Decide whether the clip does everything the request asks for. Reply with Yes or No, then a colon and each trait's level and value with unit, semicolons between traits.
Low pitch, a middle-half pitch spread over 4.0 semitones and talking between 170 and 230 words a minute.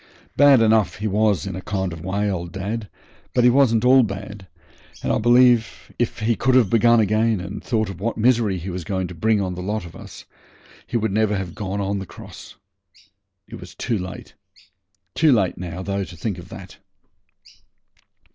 No: low, 105 Hz; average, 3.4 semitones; average, 195 wpm